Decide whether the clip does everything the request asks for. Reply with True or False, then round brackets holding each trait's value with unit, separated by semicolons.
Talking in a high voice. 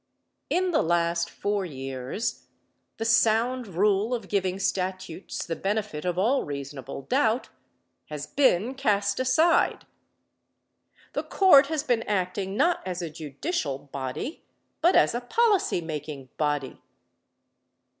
True (195 Hz)